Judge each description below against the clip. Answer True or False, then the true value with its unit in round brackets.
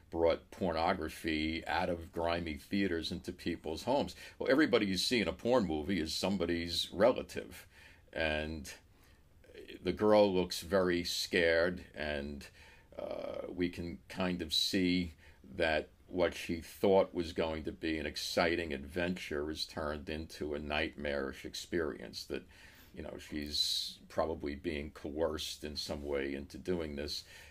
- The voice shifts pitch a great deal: False (3.0 semitones)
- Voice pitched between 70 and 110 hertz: True (85 Hz)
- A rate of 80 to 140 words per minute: True (135 wpm)